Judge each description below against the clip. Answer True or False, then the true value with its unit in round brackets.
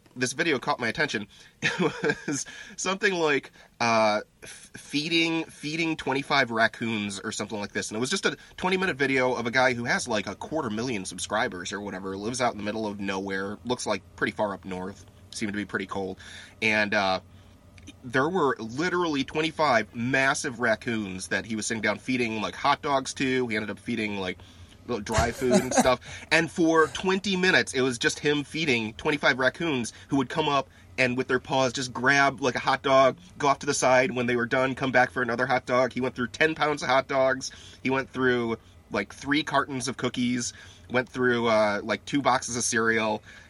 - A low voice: True (125 Hz)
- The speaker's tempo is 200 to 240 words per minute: True (205 wpm)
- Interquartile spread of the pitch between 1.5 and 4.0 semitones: False (4.7 semitones)